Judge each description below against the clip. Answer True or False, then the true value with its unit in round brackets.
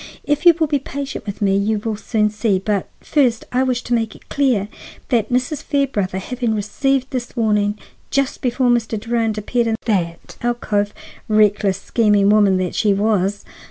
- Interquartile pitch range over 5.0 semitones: False (3.4 semitones)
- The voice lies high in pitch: True (220 Hz)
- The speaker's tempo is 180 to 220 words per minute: False (170 wpm)